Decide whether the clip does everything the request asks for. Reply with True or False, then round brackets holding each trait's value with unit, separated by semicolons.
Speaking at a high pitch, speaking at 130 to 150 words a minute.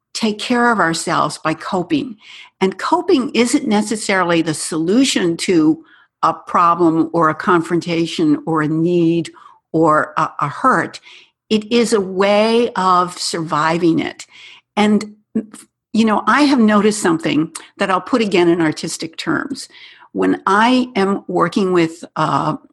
True (195 Hz; 140 wpm)